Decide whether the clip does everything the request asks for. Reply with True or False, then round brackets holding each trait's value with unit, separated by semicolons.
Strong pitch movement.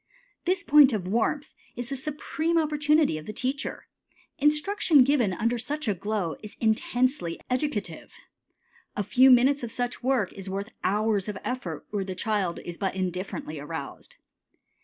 True (6.7 semitones)